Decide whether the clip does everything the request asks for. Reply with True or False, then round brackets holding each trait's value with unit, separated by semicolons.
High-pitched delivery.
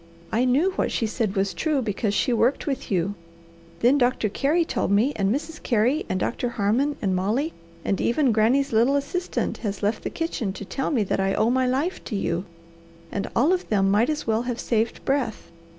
True (235 Hz)